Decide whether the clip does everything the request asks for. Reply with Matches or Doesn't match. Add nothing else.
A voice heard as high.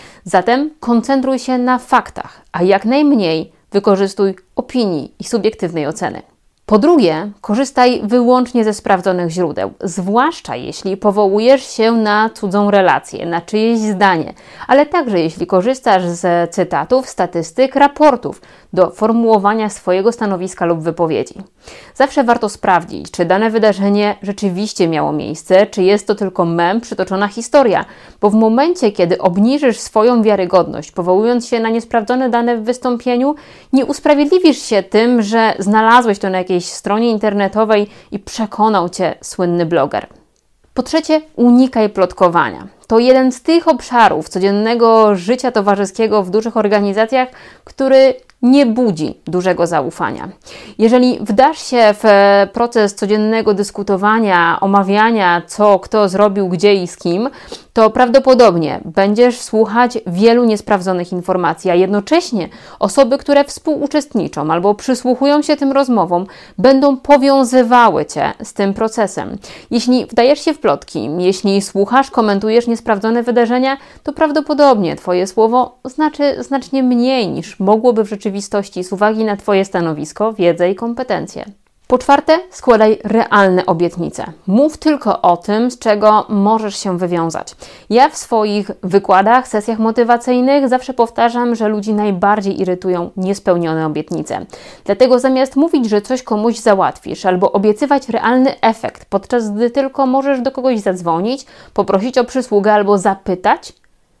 Matches